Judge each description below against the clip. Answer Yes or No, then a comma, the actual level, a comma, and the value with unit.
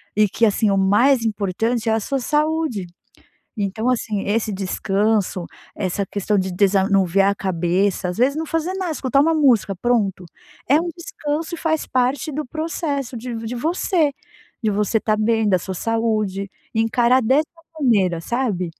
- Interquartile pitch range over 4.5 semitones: Yes, wide, 5.5 semitones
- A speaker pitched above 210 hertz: Yes, high, 225 Hz